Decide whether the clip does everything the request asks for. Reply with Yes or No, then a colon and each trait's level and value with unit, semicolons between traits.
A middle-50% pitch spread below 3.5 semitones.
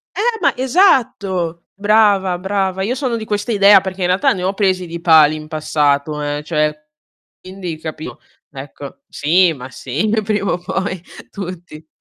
No: average, 4.5 semitones